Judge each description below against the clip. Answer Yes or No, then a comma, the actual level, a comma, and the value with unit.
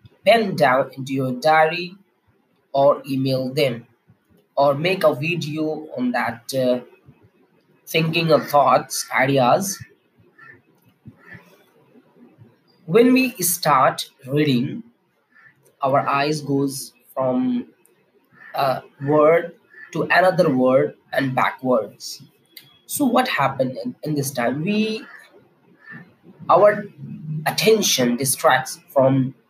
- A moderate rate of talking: No, slow, 95 wpm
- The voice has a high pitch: No, medium, 150 Hz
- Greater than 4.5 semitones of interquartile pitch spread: Yes, wide, 5.4 semitones